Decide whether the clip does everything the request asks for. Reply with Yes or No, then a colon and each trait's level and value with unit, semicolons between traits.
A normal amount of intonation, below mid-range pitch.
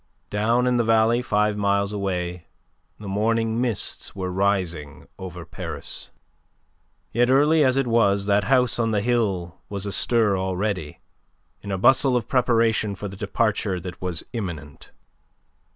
Yes: average, 3.7 semitones; low, 105 Hz